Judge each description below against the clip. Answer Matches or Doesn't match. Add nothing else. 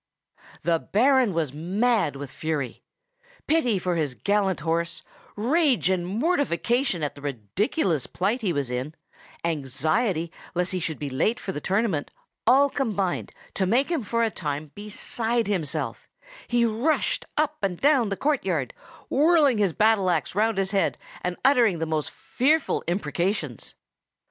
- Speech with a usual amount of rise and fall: Doesn't match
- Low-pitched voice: Doesn't match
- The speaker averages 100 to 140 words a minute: Doesn't match